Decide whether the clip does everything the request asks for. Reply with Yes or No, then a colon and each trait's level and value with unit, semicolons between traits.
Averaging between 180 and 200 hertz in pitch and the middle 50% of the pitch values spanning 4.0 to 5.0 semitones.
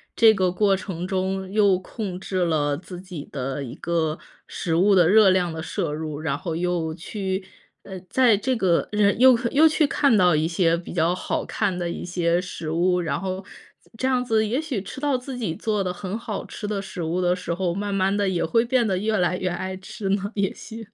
No: medium, 185 Hz; average, 3.4 semitones